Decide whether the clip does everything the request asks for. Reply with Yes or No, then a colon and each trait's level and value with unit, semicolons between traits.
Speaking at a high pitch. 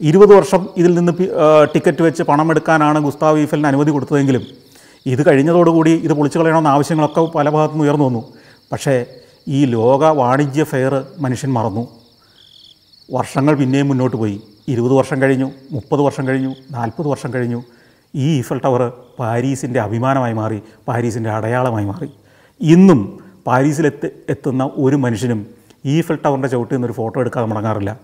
No: low, 135 Hz